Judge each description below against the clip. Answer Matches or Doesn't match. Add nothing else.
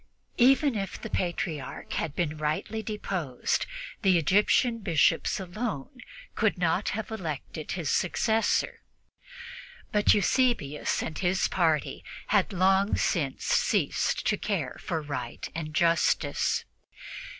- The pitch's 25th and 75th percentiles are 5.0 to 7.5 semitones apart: Matches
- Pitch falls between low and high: Matches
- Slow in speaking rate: Matches